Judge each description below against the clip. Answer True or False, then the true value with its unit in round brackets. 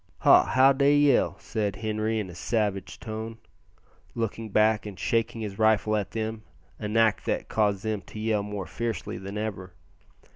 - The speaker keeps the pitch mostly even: True (1.5 semitones)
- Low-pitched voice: True (110 Hz)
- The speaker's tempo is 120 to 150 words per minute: False (170 wpm)